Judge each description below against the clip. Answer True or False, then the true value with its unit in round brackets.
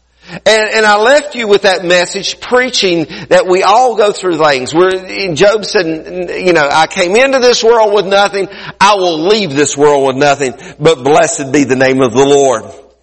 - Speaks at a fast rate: False (195 wpm)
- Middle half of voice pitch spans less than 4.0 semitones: False (4.8 semitones)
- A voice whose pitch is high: False (180 Hz)